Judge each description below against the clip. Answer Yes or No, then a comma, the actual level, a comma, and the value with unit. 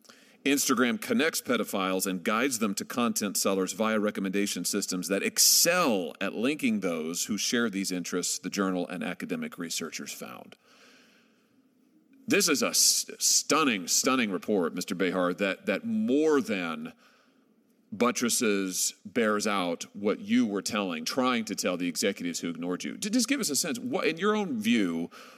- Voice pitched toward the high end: Yes, high, 225 Hz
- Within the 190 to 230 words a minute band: No, average, 155 wpm